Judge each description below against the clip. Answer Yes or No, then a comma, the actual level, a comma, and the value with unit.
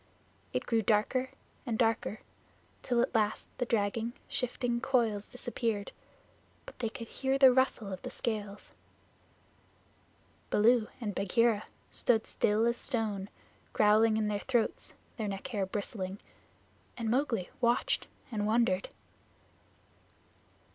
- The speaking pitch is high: Yes, high, 225 Hz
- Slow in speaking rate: Yes, slow, 120 wpm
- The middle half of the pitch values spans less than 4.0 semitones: Yes, narrow, 2.5 semitones